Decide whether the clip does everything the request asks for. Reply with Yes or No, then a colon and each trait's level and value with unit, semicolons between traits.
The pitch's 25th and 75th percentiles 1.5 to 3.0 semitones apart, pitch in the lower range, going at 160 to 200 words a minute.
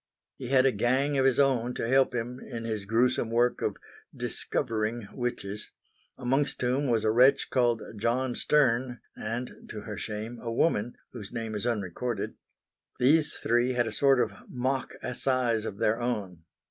Yes: narrow, 2.5 semitones; low, 120 Hz; average, 165 wpm